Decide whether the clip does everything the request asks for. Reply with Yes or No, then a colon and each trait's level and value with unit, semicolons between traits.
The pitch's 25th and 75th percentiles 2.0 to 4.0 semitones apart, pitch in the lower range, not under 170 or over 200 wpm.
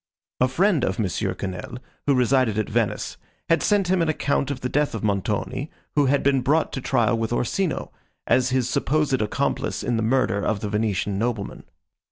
No: average, 4.6 semitones; low, 125 Hz; average, 190 wpm